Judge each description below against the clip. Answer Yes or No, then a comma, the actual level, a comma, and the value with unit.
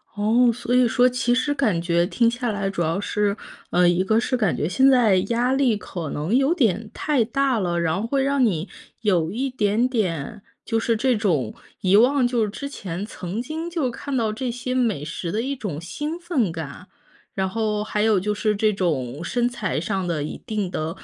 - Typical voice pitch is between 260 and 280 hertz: No, high, 215 Hz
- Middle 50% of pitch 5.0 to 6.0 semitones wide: Yes, wide, 5.4 semitones